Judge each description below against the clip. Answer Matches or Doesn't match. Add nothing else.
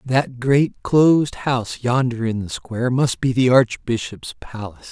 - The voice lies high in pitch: Doesn't match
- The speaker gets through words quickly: Doesn't match